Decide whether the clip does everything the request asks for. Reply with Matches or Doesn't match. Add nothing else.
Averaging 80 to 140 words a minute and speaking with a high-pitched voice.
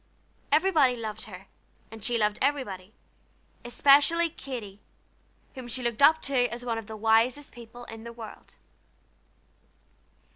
Matches